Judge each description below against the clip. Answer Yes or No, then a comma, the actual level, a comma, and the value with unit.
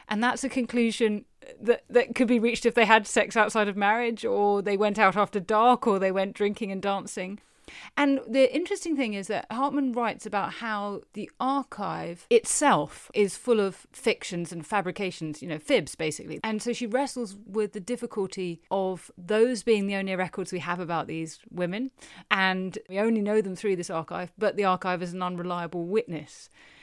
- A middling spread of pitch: Yes, average, 4.0 semitones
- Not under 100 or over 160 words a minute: No, average, 190 wpm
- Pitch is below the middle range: No, high, 205 Hz